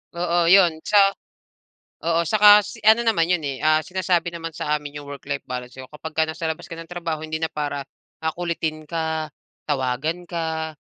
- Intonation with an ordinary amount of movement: No, narrow, 2.3 semitones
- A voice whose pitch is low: No, medium, 160 Hz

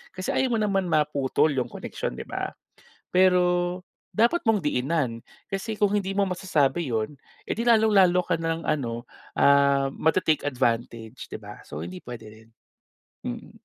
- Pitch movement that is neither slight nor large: No, wide, 7.3 semitones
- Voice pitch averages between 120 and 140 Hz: No, medium, 160 Hz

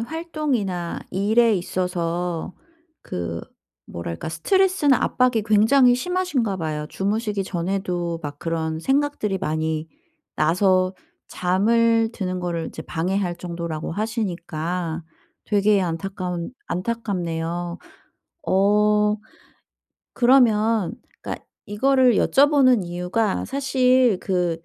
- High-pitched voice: Yes, high, 195 Hz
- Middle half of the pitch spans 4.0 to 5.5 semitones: Yes, average, 5.1 semitones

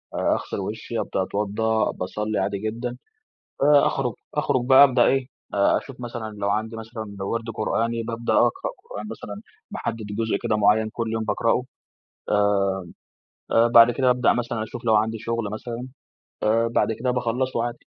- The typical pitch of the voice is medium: No, low, 115 Hz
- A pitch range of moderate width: No, narrow, 2.0 semitones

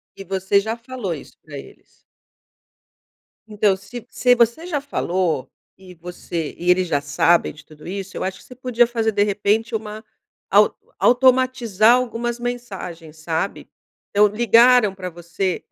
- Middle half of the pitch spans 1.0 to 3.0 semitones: No, average, 5.0 semitones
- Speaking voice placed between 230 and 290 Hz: No, high, 205 Hz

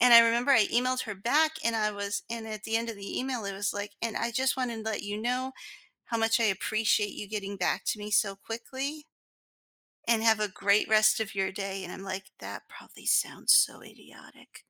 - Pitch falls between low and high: No, high, 220 Hz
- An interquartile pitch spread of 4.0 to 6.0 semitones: No, narrow, 2.5 semitones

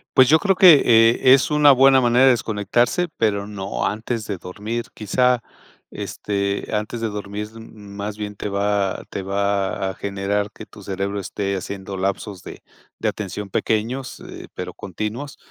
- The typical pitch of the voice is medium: No, low, 105 Hz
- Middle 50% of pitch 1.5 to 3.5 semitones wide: Yes, average, 3.1 semitones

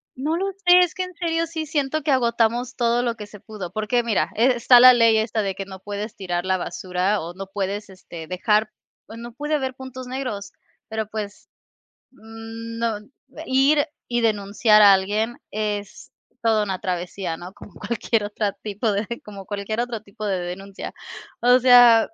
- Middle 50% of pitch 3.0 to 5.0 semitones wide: Yes, average, 3.5 semitones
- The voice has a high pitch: Yes, high, 220 Hz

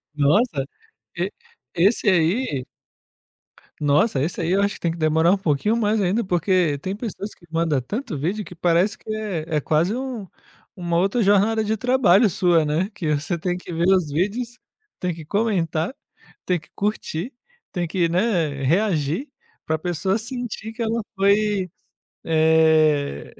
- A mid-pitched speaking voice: Yes, medium, 180 Hz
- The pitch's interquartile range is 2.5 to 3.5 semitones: No, average, 4.8 semitones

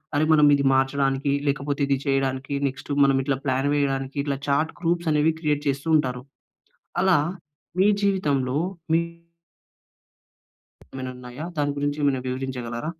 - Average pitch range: No, narrow, 1.9 semitones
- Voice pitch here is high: No, medium, 140 Hz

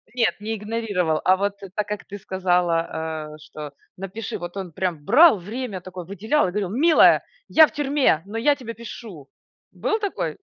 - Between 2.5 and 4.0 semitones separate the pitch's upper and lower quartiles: No, average, 4.6 semitones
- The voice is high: Yes, high, 200 Hz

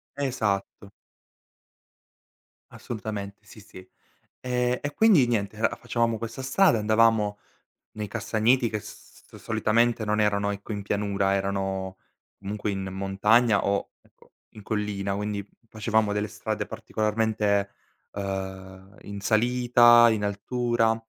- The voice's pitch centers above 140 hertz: No, low, 105 Hz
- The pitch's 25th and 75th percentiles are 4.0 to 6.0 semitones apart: No, narrow, 2.5 semitones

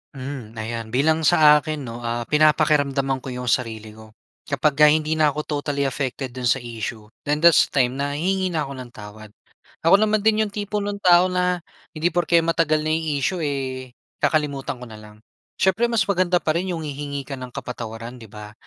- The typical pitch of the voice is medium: Yes, medium, 145 Hz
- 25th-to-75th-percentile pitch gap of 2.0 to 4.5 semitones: No, average, 5.1 semitones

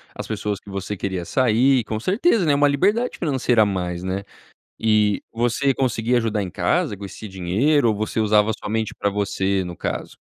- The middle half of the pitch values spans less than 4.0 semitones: No, average, 4.5 semitones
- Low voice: Yes, low, 110 Hz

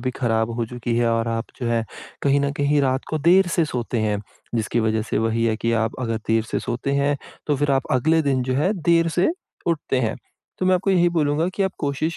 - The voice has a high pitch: No, low, 130 Hz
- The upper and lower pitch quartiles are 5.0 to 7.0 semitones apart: Yes, average, 5.3 semitones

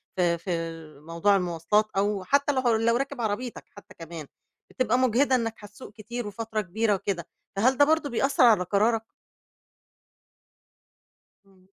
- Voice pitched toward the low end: No, high, 215 Hz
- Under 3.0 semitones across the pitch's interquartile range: No, average, 4.1 semitones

